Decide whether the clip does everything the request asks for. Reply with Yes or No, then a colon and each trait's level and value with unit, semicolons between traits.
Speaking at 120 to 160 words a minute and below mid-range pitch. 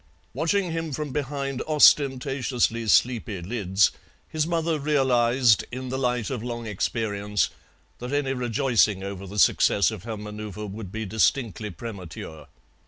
Yes: slow, 135 wpm; low, 120 Hz